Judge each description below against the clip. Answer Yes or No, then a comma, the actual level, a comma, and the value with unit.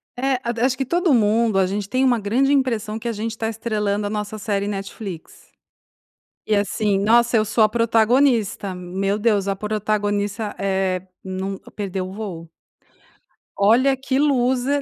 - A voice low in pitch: No, high, 215 Hz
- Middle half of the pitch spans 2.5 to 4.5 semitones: Yes, average, 3.1 semitones